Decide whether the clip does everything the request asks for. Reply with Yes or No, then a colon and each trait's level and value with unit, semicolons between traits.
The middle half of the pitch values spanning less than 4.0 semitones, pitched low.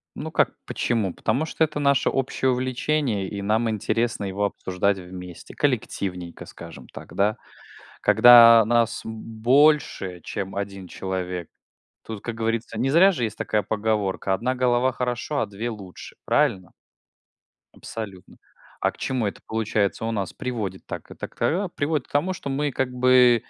No: average, 4.4 semitones; low, 115 Hz